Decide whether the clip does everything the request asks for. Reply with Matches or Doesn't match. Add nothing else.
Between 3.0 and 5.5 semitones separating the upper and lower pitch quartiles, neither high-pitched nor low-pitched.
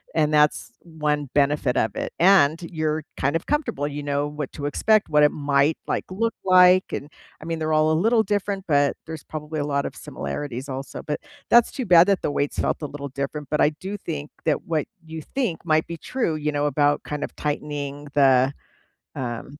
Doesn't match